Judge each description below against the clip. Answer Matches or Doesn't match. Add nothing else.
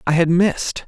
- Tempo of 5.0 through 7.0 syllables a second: Matches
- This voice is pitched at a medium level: Matches